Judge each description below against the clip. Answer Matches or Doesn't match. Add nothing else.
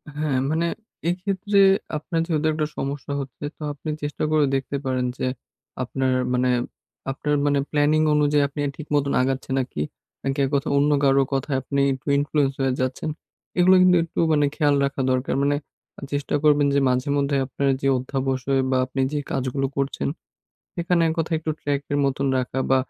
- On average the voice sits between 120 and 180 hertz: Matches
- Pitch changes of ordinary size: Doesn't match